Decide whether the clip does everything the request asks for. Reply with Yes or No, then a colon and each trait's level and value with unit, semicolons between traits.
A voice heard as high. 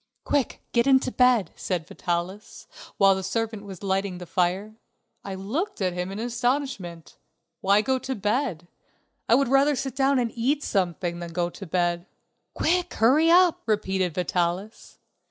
Yes: high, 205 Hz